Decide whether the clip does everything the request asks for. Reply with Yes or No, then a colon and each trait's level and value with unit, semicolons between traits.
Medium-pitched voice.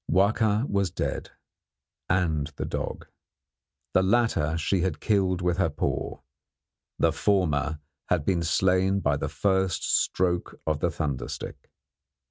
No: very low, 90 Hz